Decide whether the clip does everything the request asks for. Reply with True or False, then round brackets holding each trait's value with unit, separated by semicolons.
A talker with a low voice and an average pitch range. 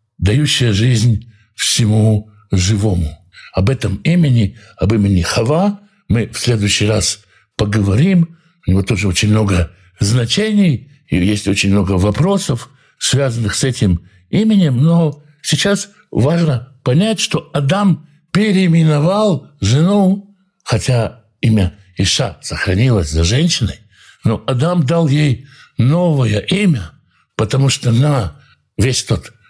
False (125 Hz; 7.5 semitones)